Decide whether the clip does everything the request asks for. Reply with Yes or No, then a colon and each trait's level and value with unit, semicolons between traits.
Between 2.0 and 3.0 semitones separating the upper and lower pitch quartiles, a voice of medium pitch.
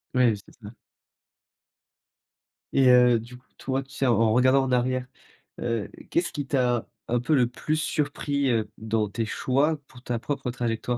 No: average, 2.7 semitones; low, 125 Hz